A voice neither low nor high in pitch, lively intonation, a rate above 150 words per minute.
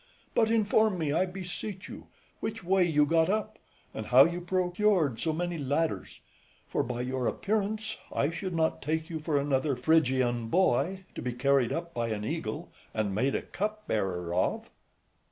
Yes: medium, 160 Hz; wide, 6.4 semitones; average, 170 wpm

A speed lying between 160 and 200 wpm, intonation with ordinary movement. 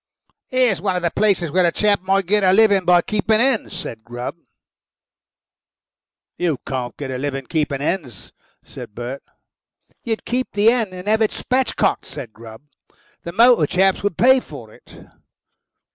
No: average, 170 wpm; wide, 7.3 semitones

